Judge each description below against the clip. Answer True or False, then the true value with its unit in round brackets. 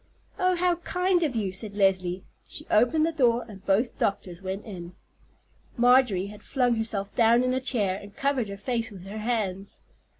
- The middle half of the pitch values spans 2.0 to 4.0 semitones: False (4.5 semitones)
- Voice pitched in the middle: False (225 Hz)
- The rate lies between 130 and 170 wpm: False (180 wpm)